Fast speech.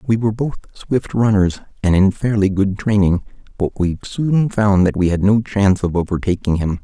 No: average, 195 wpm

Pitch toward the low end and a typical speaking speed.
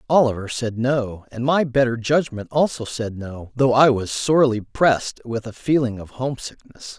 Yes: low, 125 Hz; average, 170 wpm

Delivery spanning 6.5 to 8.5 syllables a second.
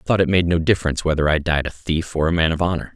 Yes: 7.4 syllables/s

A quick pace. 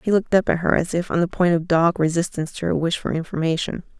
Yes: fast, 270 wpm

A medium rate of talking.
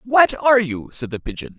No: fast, 230 wpm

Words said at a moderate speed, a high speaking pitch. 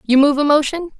No: fast, 240 wpm; very high, 290 Hz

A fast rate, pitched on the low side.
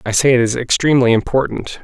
No: average, 195 wpm; low, 125 Hz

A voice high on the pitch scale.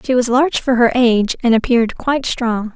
Yes: high, 240 Hz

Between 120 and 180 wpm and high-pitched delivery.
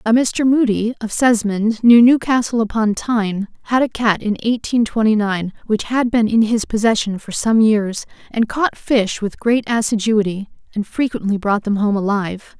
Yes: average, 175 wpm; high, 220 Hz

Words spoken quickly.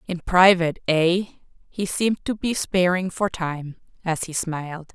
No: average, 145 wpm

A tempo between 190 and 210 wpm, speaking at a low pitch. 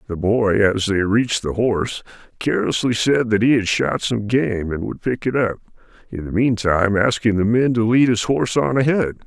Yes: fast, 205 wpm; low, 110 Hz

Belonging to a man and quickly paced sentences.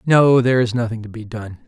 Yes: male; fast, 250 wpm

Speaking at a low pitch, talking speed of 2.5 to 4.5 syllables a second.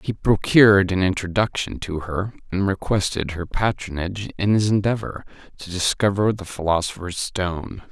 No: very low, 95 Hz; 5.0 syllables/s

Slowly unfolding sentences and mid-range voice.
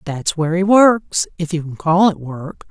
No: average, 200 wpm; medium, 170 Hz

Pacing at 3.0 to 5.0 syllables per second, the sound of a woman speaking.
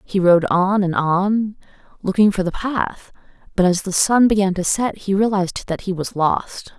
Yes: 4.5 syllables/s; female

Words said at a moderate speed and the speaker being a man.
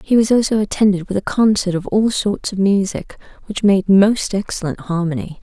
No: average, 190 wpm; female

